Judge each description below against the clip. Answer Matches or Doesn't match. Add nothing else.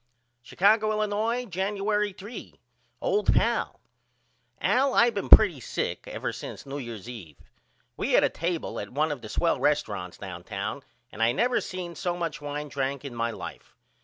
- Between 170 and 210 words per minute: Doesn't match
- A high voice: Doesn't match